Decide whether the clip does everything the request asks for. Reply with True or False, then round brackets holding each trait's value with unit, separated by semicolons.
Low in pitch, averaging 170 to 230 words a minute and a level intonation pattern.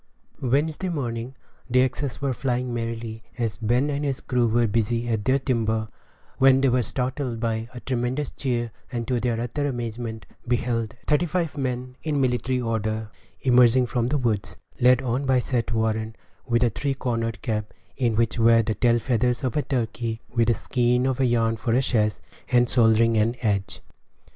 True (120 Hz; 175 wpm; 2.2 semitones)